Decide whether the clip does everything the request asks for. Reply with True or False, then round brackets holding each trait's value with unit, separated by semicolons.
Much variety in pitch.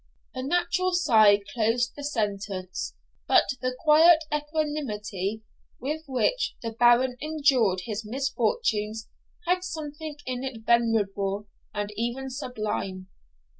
True (6.0 semitones)